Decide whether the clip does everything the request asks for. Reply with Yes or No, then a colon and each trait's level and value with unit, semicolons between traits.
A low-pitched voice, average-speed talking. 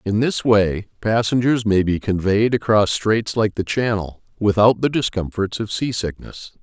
Yes: low, 105 Hz; average, 165 wpm